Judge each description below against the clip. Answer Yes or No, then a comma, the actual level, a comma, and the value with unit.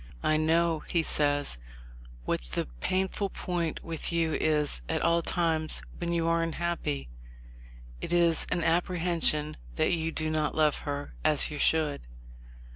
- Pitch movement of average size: No, narrow, 1.9 semitones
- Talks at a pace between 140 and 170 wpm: Yes, average, 150 wpm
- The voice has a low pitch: No, medium, 160 Hz